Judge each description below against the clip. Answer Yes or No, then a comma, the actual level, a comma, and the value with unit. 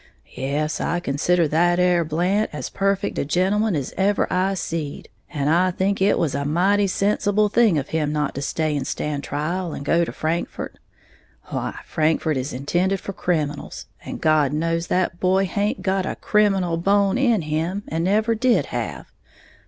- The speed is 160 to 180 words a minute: Yes, average, 175 wpm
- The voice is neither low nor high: Yes, medium, 175 Hz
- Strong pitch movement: No, average, 4.3 semitones